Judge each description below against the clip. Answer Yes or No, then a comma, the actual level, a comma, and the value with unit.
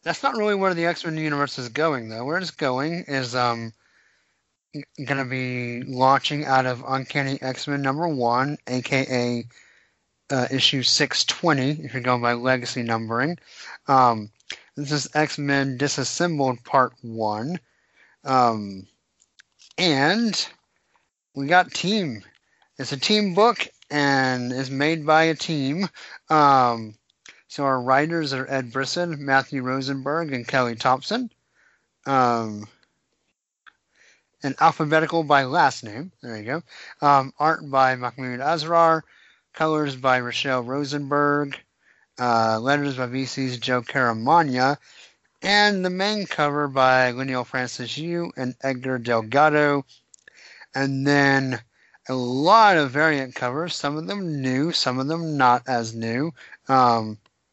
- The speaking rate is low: Yes, slow, 130 wpm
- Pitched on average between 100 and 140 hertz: Yes, low, 135 Hz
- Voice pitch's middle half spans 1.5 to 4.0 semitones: Yes, average, 3.3 semitones